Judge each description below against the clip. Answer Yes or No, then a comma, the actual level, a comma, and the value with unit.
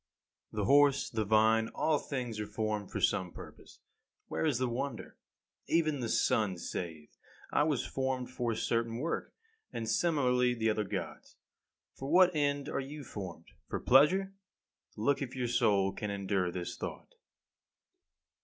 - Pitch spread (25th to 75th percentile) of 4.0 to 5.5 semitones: Yes, average, 4.8 semitones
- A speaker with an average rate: Yes, average, 155 wpm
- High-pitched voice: No, low, 120 Hz